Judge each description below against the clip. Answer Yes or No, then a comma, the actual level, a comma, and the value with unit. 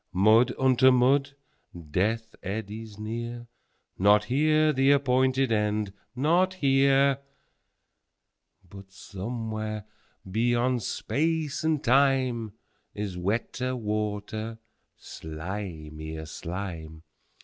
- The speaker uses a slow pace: Yes, slow, 75 wpm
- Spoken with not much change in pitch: No, average, 4.7 semitones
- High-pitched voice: No, low, 115 Hz